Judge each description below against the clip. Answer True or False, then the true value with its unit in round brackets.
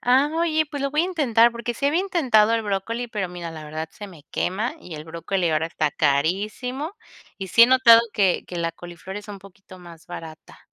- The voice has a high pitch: True (205 Hz)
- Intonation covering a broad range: True (6.5 semitones)